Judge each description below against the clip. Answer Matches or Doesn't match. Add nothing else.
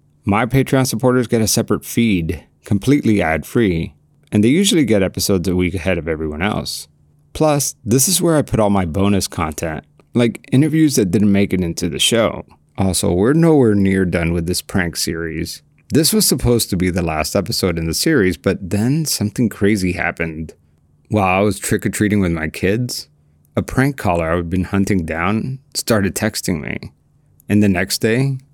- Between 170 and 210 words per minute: Matches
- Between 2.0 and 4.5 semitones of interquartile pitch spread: Doesn't match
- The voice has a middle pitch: Doesn't match